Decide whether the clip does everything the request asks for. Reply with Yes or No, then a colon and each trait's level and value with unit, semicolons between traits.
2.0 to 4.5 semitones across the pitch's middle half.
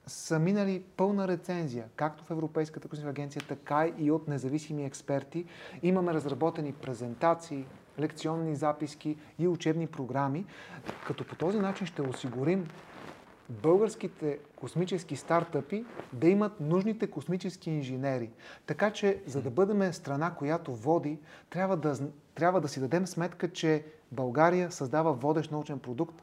Yes: average, 3.5 semitones